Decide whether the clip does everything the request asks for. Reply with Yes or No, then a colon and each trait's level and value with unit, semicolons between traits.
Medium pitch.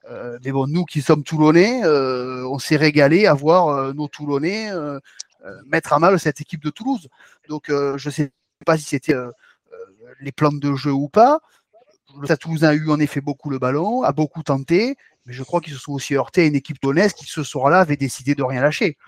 Yes: medium, 150 Hz